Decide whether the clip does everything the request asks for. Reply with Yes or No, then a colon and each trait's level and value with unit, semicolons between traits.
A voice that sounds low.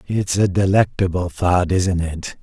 Yes: very low, 90 Hz